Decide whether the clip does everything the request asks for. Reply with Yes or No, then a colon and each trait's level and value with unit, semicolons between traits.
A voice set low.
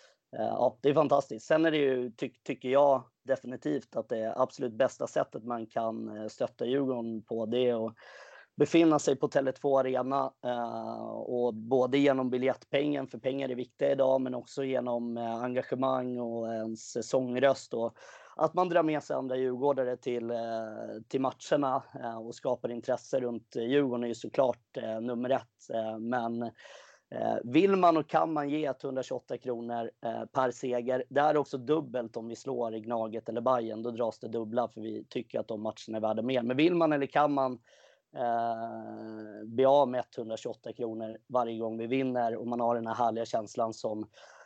Yes: low, 125 Hz